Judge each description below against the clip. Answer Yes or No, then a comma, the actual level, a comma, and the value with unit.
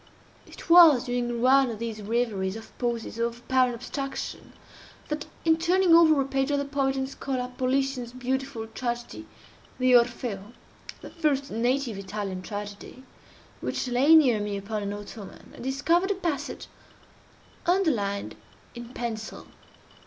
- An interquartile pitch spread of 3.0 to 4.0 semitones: Yes, average, 3.7 semitones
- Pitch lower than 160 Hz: No, very high, 250 Hz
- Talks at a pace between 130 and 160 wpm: Yes, average, 140 wpm